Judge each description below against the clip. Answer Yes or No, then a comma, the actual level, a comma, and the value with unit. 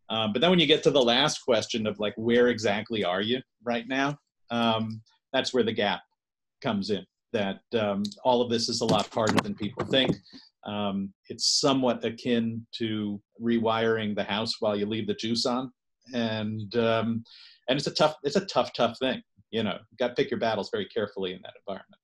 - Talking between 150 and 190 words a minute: No, fast, 205 wpm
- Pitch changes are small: Yes, narrow, 2.1 semitones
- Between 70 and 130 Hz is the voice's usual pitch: Yes, low, 115 Hz